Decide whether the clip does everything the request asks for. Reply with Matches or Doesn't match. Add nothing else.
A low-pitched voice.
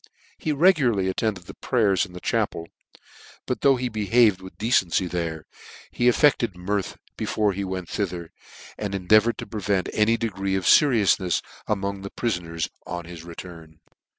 Matches